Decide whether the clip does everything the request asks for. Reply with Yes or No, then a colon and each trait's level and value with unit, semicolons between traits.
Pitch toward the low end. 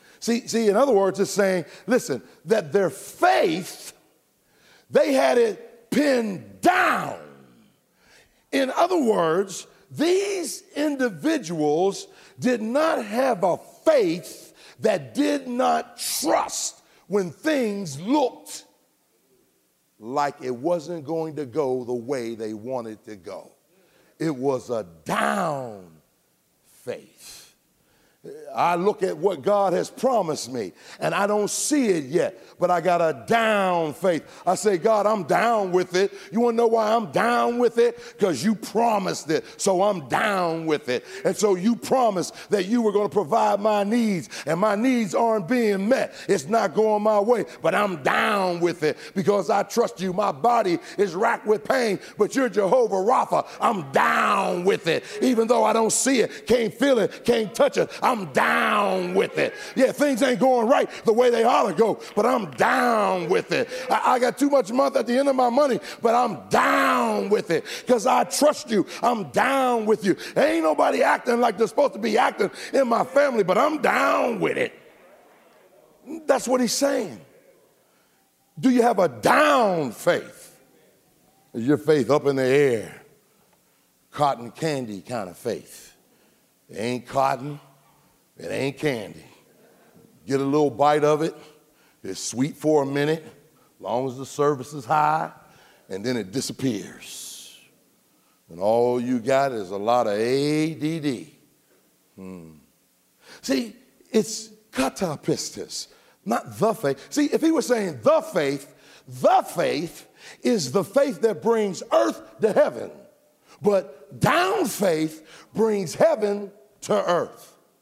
No: high, 205 Hz